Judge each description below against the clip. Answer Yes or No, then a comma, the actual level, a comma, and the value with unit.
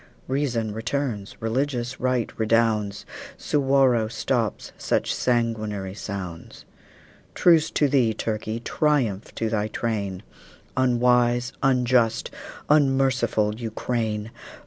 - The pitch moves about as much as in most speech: Yes, average, 3.2 semitones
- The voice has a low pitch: Yes, low, 115 Hz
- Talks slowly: Yes, slow, 90 wpm